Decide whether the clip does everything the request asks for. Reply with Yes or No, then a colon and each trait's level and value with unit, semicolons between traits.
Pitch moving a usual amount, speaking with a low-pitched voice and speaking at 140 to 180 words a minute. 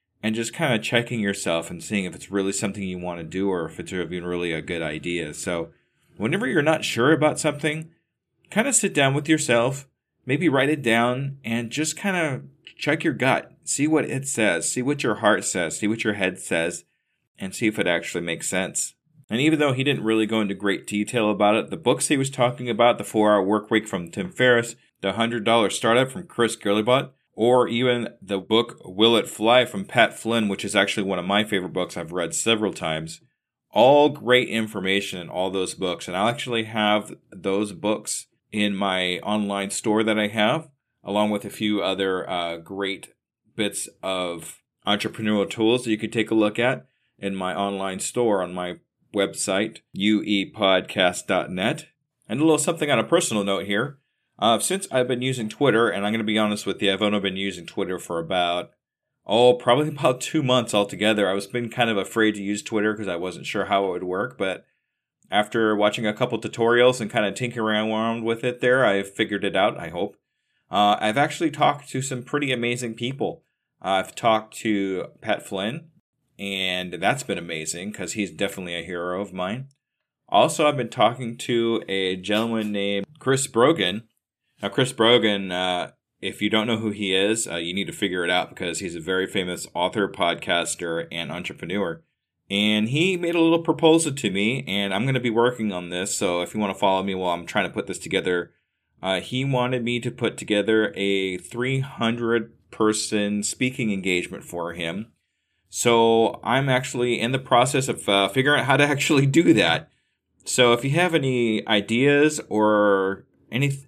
No: average, 4.1 semitones; low, 110 Hz; average, 195 wpm